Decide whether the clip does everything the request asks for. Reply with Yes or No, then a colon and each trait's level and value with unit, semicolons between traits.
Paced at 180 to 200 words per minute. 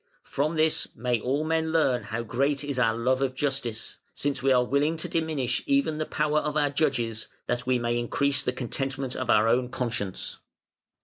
Yes: average, 190 wpm